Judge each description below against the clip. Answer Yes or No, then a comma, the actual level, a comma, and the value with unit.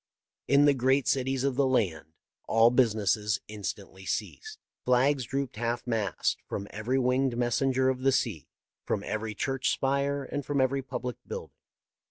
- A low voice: Yes, low, 125 Hz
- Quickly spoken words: No, average, 160 wpm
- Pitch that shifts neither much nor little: Yes, average, 3.4 semitones